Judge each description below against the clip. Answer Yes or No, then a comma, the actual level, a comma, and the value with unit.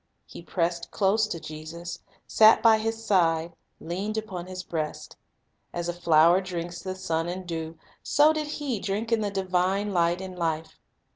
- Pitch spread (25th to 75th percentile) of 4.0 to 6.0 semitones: No, average, 3.6 semitones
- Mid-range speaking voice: Yes, medium, 180 Hz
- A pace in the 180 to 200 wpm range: No, average, 165 wpm